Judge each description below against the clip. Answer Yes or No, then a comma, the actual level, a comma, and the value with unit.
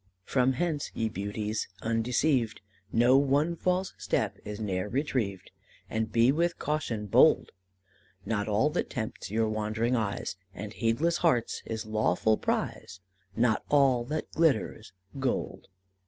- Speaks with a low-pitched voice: Yes, low, 115 Hz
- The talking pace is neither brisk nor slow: No, slow, 130 wpm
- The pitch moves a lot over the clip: No, average, 4.6 semitones